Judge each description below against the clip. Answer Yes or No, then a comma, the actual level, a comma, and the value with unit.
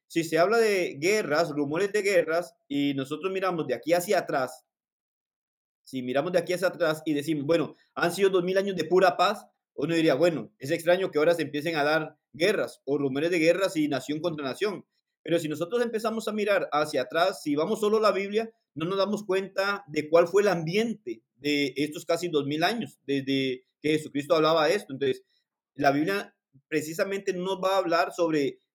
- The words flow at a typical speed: No, fast, 200 wpm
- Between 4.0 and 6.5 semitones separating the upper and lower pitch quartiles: Yes, average, 4.4 semitones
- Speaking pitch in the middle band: Yes, medium, 170 Hz